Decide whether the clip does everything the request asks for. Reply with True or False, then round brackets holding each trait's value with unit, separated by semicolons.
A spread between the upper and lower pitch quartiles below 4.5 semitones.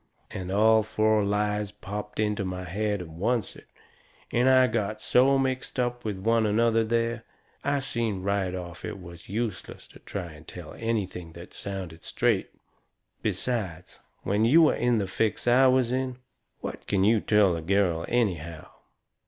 True (4.0 semitones)